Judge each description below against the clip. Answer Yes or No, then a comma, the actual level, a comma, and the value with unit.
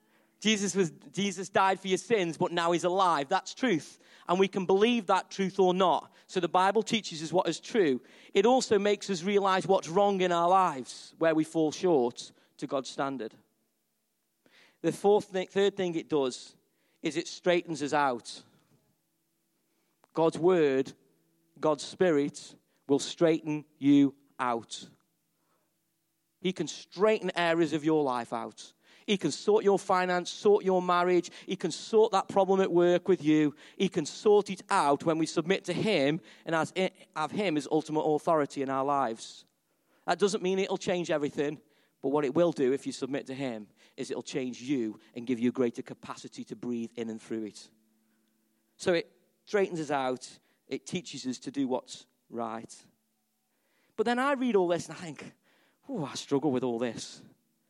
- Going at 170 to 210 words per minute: Yes, average, 175 wpm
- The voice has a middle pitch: Yes, medium, 170 Hz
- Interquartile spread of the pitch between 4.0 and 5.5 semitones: Yes, average, 5.1 semitones